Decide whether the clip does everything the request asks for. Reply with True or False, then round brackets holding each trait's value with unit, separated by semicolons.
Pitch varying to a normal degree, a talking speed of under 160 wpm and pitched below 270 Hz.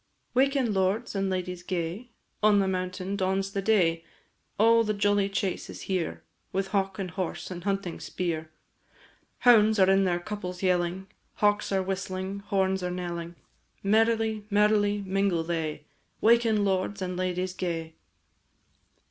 False (2.2 semitones; 140 wpm; 190 Hz)